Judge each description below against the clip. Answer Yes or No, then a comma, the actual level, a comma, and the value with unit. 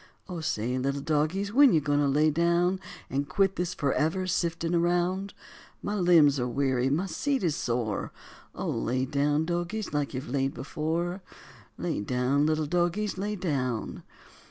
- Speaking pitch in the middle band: Yes, medium, 155 Hz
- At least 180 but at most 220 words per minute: No, average, 155 wpm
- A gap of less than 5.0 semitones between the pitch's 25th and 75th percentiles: Yes, average, 4.3 semitones